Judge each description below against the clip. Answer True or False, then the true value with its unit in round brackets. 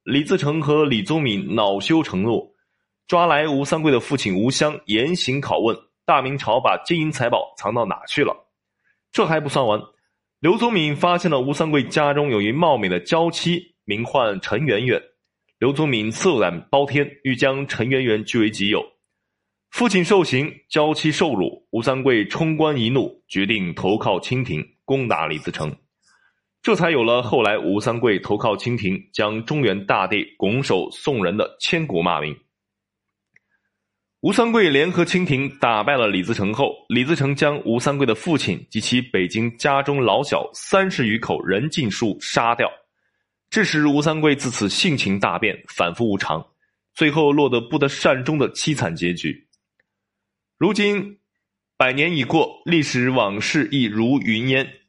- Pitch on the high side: False (140 Hz)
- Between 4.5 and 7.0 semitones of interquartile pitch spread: True (5.5 semitones)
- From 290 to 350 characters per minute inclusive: False (240 characters per minute)